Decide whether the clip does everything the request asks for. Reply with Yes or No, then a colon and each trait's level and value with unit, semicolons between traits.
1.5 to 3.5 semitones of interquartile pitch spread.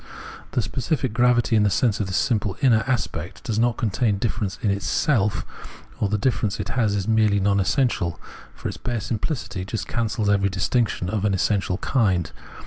Yes: average, 3.2 semitones